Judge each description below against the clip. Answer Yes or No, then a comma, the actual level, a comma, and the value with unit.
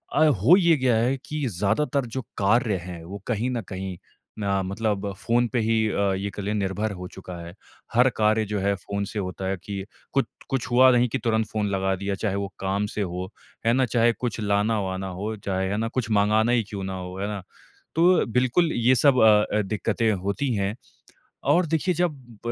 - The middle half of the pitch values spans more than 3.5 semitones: Yes, average, 3.9 semitones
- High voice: No, low, 105 Hz